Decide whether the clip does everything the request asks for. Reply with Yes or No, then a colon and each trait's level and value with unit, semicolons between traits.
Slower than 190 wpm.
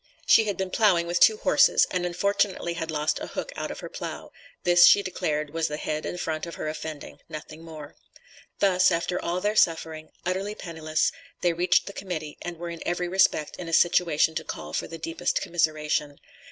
No: average, 200 wpm